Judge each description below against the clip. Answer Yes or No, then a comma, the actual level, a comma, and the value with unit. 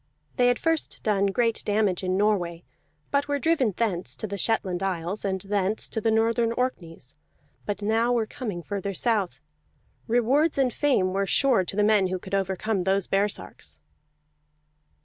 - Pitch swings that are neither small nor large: Yes, average, 3.5 semitones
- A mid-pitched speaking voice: No, high, 205 Hz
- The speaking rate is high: No, average, 165 wpm